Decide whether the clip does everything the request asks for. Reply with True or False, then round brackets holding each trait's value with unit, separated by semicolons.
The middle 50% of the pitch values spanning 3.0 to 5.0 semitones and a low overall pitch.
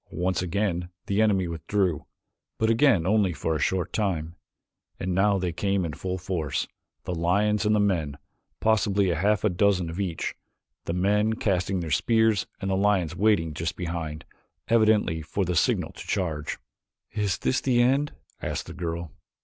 True (3.7 semitones; 95 Hz)